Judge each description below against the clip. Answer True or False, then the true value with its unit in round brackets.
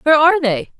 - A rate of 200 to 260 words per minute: True (225 wpm)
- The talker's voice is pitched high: True (295 Hz)